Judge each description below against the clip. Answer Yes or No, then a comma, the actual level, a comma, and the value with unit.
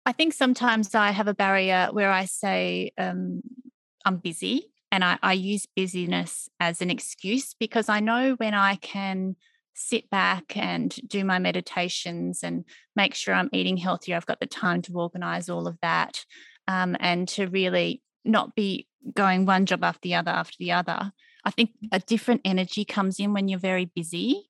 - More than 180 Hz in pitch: Yes, high, 190 Hz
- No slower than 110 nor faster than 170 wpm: No, average, 180 wpm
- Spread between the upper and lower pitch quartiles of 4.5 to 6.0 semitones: No, average, 3.8 semitones